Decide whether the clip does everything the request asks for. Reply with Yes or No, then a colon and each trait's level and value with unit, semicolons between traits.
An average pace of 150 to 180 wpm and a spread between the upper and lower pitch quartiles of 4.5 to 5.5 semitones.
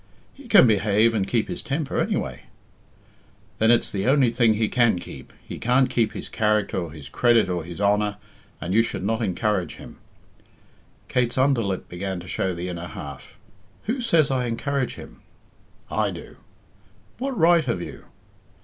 Yes: average, 170 wpm; average, 5.2 semitones